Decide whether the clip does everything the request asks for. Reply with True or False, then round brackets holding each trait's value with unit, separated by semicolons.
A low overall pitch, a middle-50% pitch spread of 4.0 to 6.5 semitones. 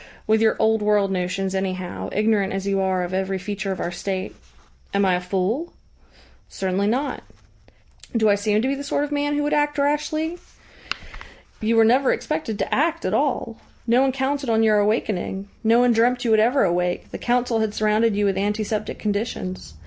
False (215 Hz; 4.3 semitones)